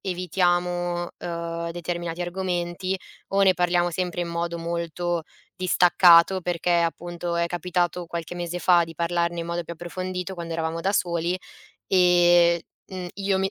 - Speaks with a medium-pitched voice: Yes, medium, 175 Hz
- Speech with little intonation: Yes, narrow, 0.9 semitones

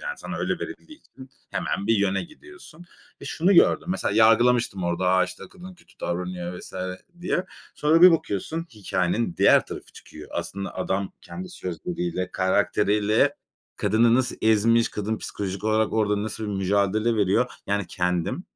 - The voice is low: Yes, low, 110 Hz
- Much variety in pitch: Yes, wide, 7.4 semitones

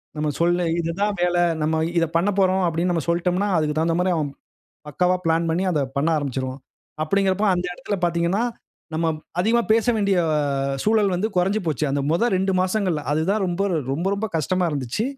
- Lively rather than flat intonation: No, average, 3.3 semitones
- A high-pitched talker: No, medium, 175 Hz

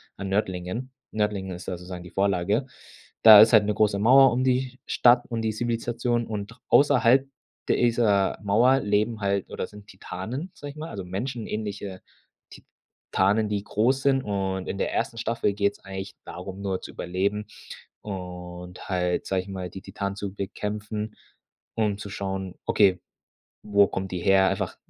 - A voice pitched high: No, low, 100 Hz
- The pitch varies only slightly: No, average, 3.2 semitones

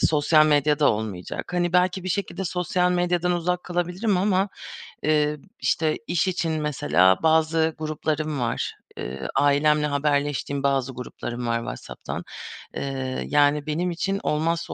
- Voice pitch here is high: No, medium, 155 Hz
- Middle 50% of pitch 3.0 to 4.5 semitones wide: Yes, average, 3.7 semitones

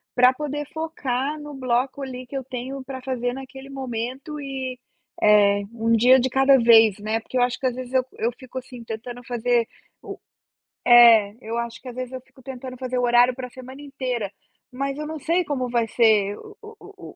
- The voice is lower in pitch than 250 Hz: No, very high, 255 Hz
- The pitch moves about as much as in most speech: No, narrow, 2.1 semitones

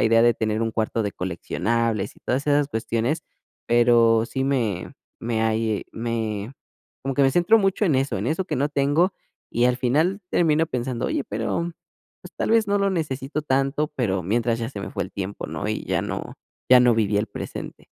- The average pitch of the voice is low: Yes, low, 120 Hz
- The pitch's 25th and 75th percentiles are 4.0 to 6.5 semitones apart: Yes, average, 4.6 semitones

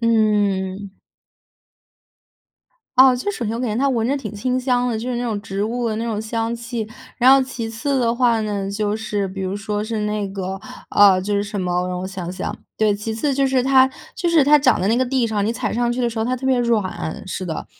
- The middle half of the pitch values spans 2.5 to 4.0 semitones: Yes, average, 3.5 semitones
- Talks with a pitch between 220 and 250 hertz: Yes, high, 225 Hz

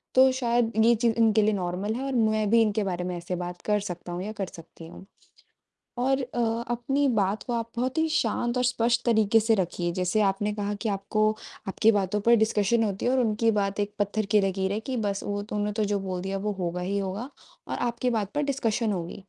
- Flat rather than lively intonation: No, average, 3.3 semitones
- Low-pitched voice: No, high, 210 Hz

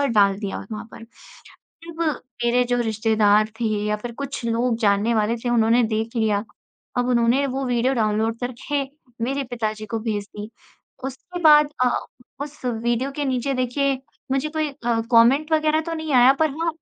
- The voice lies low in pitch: No, high, 240 Hz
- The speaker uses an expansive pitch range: No, average, 3.7 semitones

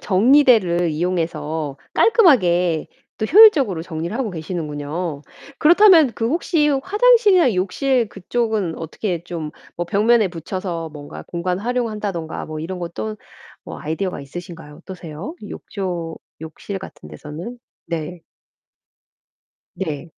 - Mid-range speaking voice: Yes, medium, 180 Hz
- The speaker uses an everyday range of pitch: No, wide, 6.4 semitones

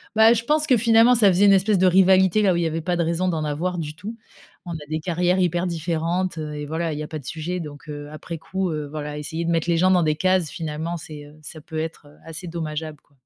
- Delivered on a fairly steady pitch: No, average, 3.2 semitones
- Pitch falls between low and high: Yes, medium, 165 Hz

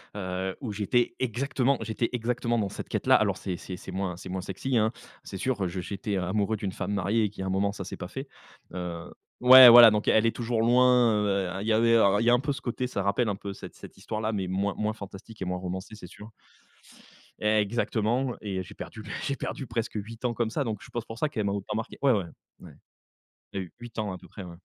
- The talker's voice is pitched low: Yes, low, 105 Hz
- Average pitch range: Yes, average, 3.6 semitones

